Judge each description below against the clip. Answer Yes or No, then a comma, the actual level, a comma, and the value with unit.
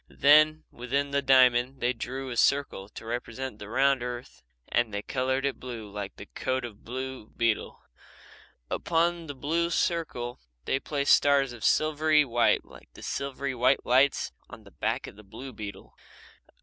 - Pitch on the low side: Yes, low, 130 Hz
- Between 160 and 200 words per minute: Yes, average, 170 wpm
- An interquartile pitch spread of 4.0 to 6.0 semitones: No, average, 2.8 semitones